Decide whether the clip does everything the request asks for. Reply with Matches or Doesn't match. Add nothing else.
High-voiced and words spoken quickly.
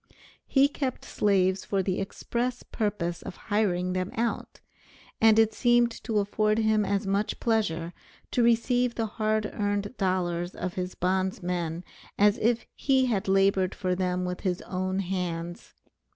Doesn't match